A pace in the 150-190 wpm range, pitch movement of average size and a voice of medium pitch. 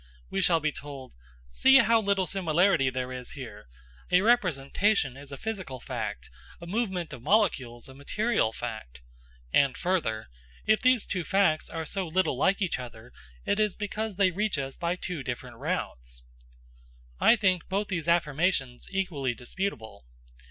No: average, 155 wpm; wide, 7.3 semitones; medium, 170 Hz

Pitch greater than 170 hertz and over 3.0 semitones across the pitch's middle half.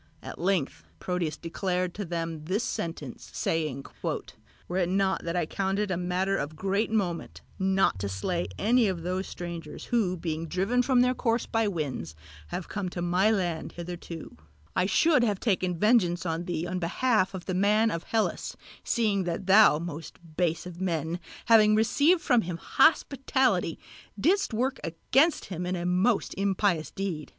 Yes: medium, 185 Hz; average, 3.9 semitones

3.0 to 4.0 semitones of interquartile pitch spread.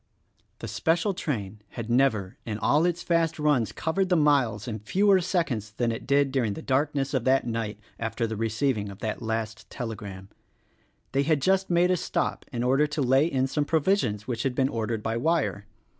No: wide, 5.5 semitones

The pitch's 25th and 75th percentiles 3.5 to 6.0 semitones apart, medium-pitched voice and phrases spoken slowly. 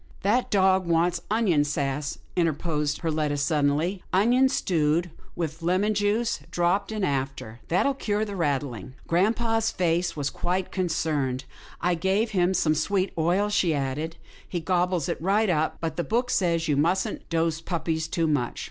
No: average, 3.9 semitones; medium, 170 Hz; average, 170 wpm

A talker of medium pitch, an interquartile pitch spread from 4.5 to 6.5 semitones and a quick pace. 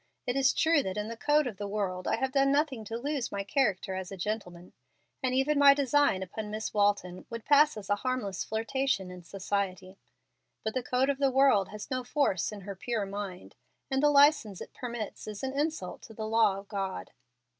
No: high, 220 Hz; average, 5.3 semitones; fast, 210 wpm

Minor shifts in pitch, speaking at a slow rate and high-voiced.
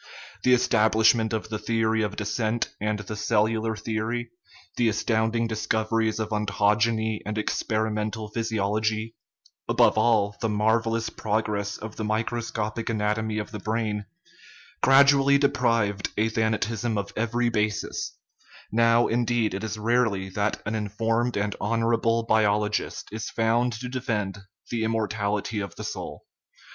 No: narrow, 1.5 semitones; slow, 130 wpm; low, 110 Hz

